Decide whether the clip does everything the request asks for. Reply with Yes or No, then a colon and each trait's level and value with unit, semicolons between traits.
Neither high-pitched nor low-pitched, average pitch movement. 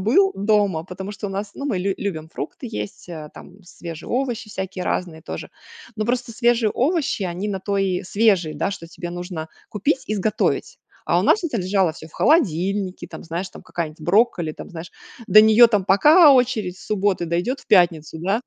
No: high, 195 Hz; average, 4.0 semitones